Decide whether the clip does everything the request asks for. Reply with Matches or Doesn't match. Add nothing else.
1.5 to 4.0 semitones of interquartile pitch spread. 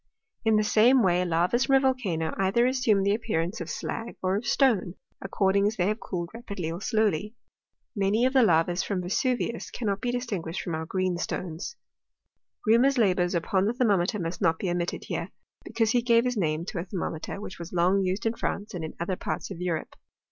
Doesn't match